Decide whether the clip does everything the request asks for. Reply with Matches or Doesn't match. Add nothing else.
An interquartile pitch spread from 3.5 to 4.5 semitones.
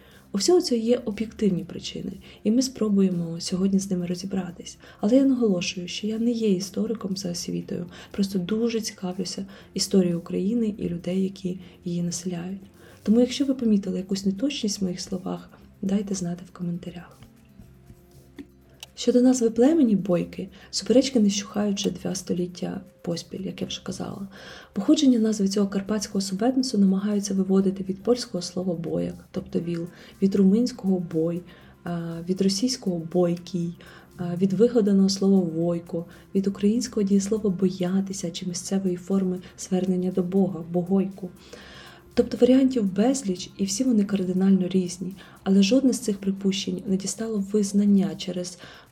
Doesn't match